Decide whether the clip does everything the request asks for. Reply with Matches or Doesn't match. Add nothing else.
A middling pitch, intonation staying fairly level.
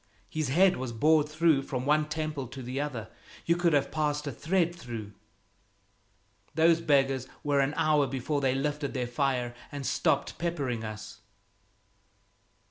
Doesn't match